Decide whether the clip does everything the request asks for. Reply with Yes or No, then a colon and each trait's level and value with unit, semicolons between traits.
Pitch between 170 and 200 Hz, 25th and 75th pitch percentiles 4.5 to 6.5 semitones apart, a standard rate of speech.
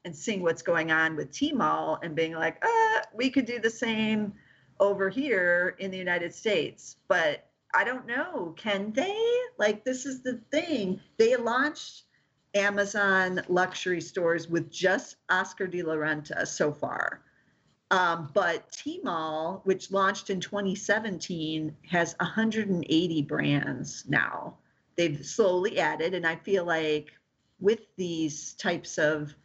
Yes: medium, 185 Hz; average, 4.8 semitones; average, 145 wpm